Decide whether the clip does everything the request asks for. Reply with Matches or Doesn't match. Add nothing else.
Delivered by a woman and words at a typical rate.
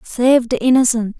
Matches